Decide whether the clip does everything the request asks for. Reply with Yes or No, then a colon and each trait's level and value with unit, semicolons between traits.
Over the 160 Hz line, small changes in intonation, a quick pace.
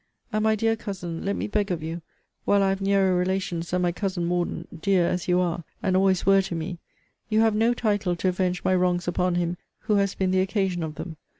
Yes: medium, 185 Hz; narrow, 2.1 semitones; fast, 230 wpm